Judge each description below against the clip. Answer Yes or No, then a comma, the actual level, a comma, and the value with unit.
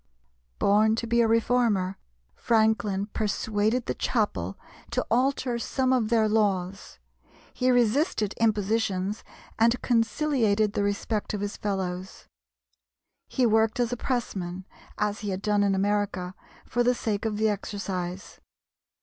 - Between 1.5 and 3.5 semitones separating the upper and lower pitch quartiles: Yes, average, 2.7 semitones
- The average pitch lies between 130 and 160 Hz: No, high, 215 Hz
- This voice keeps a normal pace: No, slow, 130 wpm